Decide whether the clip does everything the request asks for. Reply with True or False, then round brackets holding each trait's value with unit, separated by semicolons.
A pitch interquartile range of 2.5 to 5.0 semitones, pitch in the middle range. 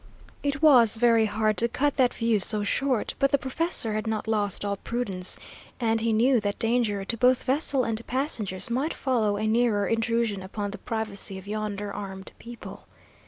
False (3.1 semitones; 225 Hz)